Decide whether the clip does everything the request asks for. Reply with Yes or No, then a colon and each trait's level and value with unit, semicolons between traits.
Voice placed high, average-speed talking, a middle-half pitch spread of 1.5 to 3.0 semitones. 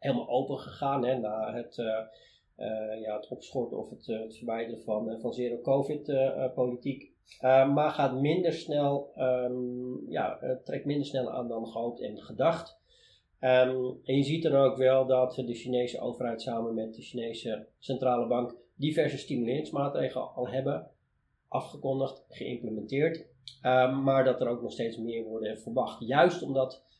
No: low, 125 Hz; average, 155 wpm; narrow, 2.5 semitones